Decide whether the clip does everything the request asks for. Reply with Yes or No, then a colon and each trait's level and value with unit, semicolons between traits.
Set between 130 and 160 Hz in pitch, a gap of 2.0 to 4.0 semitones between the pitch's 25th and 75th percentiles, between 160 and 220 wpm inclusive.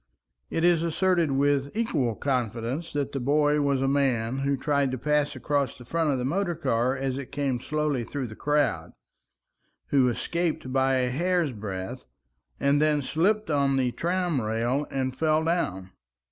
Yes: medium, 140 Hz; average, 3.2 semitones; average, 170 wpm